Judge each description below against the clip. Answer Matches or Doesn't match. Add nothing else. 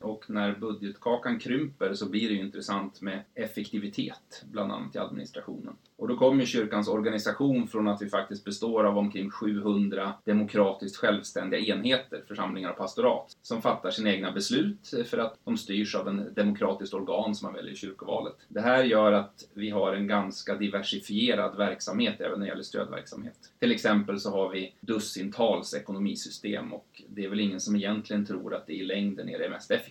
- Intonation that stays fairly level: Matches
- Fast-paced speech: Doesn't match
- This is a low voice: Matches